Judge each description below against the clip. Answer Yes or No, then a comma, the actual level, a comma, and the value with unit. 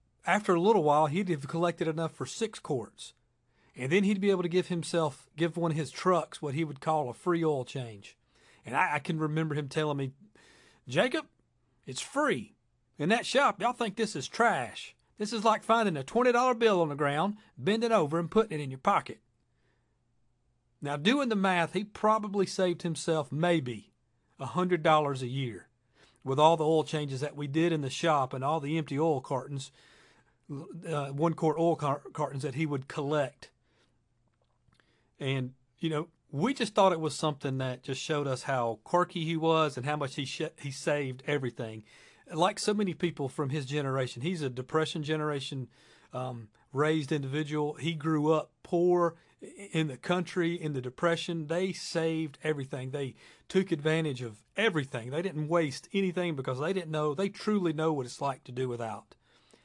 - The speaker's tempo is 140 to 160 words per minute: No, average, 185 wpm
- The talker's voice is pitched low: No, medium, 155 Hz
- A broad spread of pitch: No, average, 4.1 semitones